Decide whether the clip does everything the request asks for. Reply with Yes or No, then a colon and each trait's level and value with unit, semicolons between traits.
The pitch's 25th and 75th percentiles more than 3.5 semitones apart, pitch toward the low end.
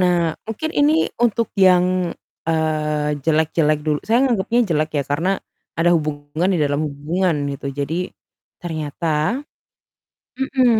No: average, 4.0 semitones; medium, 160 Hz